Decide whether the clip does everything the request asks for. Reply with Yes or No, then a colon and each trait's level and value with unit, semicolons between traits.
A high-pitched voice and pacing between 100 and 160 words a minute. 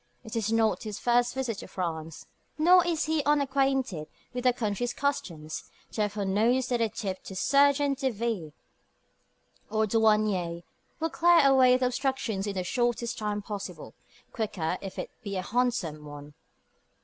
Yes: high, 225 Hz; average, 155 wpm